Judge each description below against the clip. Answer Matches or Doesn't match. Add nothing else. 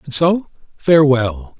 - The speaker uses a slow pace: Matches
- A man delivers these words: Matches